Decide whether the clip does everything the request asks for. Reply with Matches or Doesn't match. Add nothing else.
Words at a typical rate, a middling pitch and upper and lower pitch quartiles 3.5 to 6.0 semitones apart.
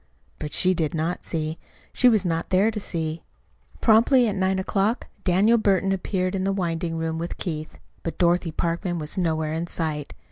Doesn't match